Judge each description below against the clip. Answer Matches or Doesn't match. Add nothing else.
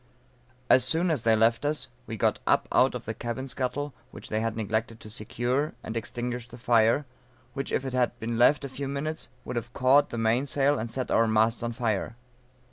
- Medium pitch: Doesn't match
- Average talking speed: Doesn't match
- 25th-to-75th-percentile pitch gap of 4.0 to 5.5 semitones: Doesn't match